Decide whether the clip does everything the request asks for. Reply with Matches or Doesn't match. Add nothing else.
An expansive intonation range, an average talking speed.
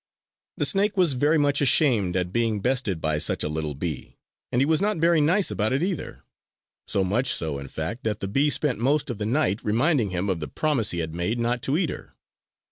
Doesn't match